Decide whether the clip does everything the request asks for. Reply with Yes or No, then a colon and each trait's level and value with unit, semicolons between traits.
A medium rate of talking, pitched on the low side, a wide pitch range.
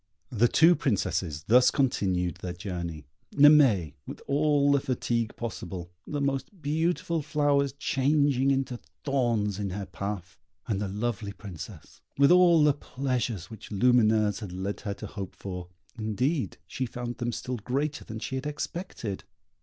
Yes: average, 150 wpm; low, 120 Hz; wide, 5.9 semitones